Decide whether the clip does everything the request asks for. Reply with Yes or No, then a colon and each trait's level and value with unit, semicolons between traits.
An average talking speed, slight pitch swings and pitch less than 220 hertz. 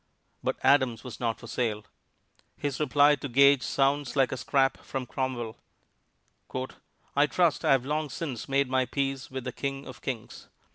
Yes: average, 170 wpm; narrow, 2.0 semitones; low, 135 Hz